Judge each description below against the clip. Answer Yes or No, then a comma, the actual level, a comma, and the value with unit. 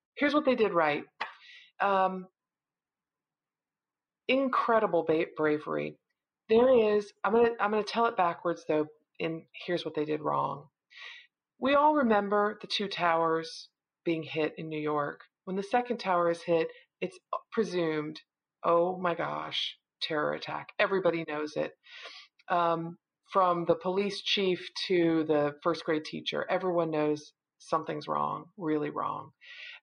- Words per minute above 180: No, slow, 135 wpm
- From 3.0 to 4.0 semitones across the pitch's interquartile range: No, average, 4.7 semitones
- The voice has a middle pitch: Yes, medium, 175 Hz